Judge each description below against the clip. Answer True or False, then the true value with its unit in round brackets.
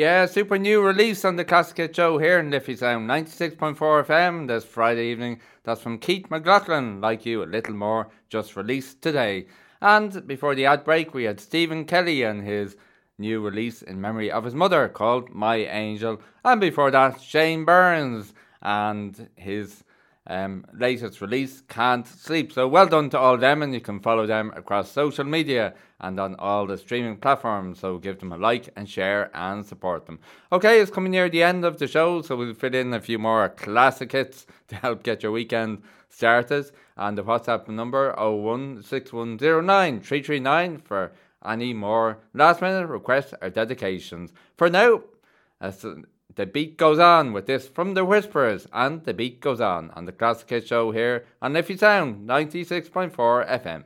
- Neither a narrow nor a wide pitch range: False (6.6 semitones)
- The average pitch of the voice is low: True (125 Hz)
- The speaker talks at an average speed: True (175 wpm)